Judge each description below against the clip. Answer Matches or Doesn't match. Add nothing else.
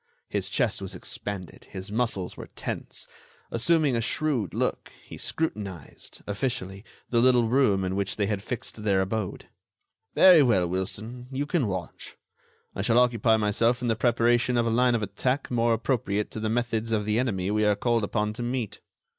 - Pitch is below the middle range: Matches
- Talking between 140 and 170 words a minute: Doesn't match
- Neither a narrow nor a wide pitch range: Matches